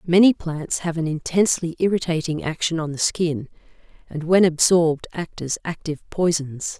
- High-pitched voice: No, medium, 165 Hz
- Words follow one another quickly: No, average, 150 wpm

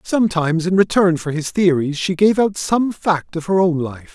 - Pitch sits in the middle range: Yes, medium, 175 Hz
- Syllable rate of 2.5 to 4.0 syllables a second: No, 4.9 syllables/s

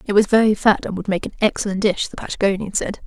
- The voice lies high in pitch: Yes, high, 200 Hz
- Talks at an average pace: No, fast, 255 wpm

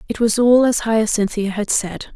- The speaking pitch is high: Yes, high, 220 Hz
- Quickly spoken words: No, average, 195 wpm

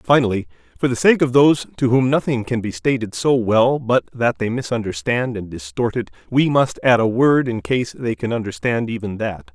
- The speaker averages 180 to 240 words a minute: Yes, fast, 205 wpm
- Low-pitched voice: Yes, low, 120 Hz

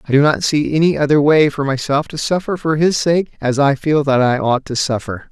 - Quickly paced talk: Yes, fast, 250 wpm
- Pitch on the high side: No, medium, 145 Hz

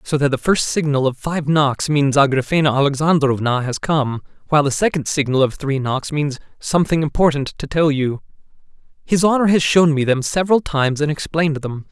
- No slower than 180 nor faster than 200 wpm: Yes, average, 185 wpm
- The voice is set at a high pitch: No, medium, 145 Hz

